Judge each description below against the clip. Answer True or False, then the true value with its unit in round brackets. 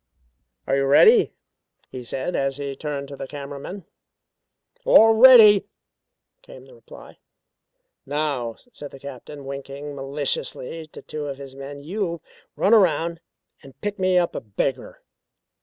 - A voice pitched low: False (145 Hz)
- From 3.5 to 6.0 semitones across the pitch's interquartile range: True (5.2 semitones)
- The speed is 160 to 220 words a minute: False (140 wpm)